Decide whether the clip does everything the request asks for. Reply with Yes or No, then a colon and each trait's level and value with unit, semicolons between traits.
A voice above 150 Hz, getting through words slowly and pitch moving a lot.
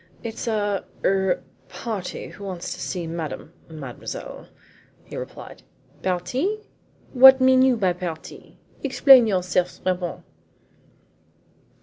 Yes: high, 190 Hz; slow, 110 wpm; wide, 5.8 semitones